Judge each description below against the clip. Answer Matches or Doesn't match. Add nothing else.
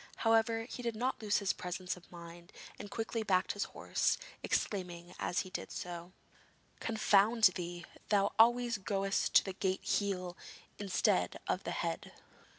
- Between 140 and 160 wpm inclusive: Matches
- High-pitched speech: Matches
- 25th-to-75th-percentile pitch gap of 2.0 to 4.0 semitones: Matches